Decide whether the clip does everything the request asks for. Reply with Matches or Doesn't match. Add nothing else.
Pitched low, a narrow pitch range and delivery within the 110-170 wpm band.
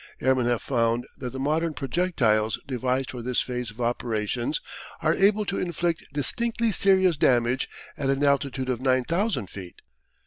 Doesn't match